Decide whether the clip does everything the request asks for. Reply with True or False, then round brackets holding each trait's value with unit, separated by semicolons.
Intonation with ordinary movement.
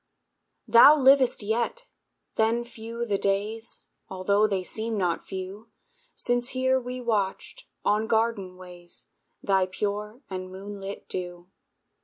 True (3.7 semitones)